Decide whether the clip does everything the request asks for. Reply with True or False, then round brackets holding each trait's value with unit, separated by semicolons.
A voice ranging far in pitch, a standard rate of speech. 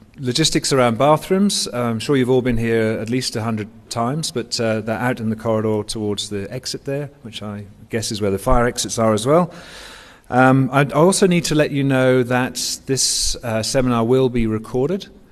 False (3.8 semitones; 195 wpm)